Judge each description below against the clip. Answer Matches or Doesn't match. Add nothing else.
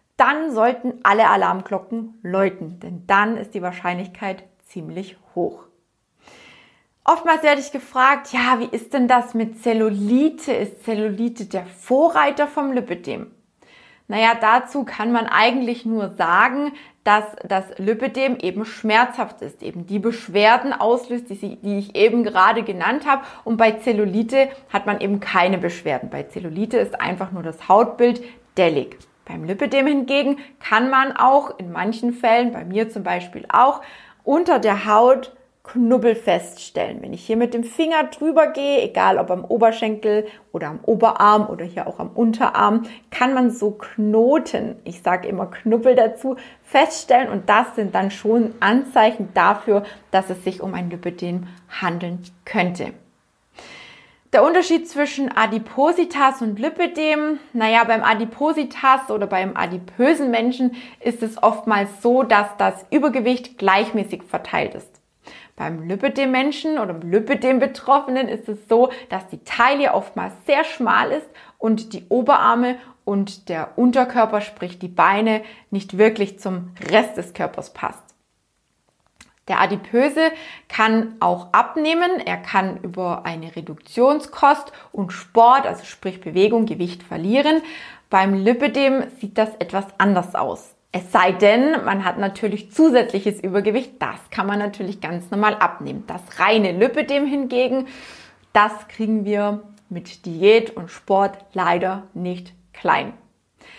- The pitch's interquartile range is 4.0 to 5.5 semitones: Matches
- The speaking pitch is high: Matches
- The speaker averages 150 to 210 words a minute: Doesn't match